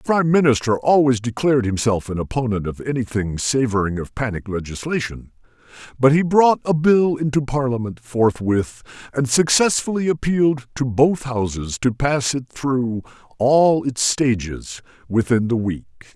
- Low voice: Yes, low, 125 Hz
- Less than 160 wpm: Yes, average, 140 wpm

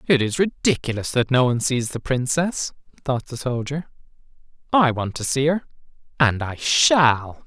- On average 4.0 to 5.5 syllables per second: Yes, 4.6 syllables/s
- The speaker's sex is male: Yes, male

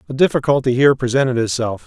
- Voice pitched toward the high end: No, low, 125 Hz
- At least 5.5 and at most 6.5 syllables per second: No, 7.1 syllables/s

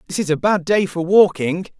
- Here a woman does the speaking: No, male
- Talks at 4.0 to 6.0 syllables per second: Yes, 5.4 syllables/s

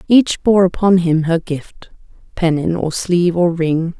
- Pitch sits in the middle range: Yes, medium, 175 Hz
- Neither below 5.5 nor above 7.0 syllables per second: No, 4.1 syllables/s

